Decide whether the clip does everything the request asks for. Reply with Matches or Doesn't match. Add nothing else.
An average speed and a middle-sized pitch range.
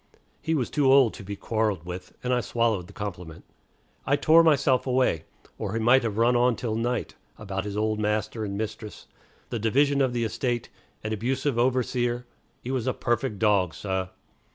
Matches